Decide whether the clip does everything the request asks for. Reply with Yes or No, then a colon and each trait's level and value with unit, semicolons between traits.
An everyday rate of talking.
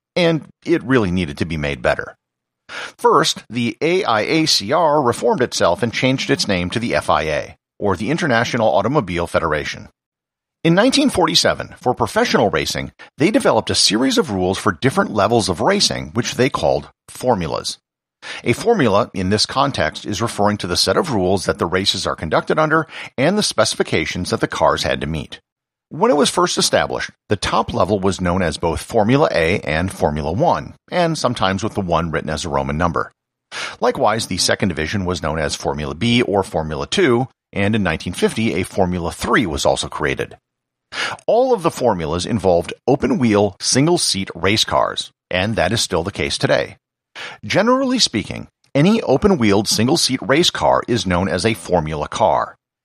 Yes: average, 175 wpm